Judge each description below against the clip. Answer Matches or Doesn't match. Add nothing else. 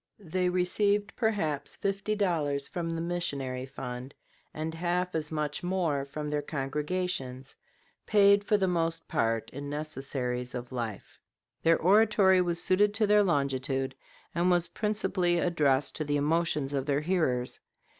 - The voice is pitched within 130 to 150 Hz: Doesn't match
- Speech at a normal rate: Matches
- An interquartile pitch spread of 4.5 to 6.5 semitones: Matches